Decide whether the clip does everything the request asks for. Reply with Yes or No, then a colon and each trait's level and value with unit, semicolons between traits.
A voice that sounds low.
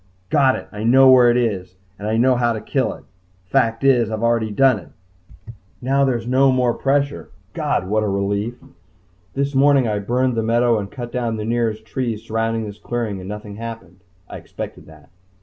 Yes: low, 115 Hz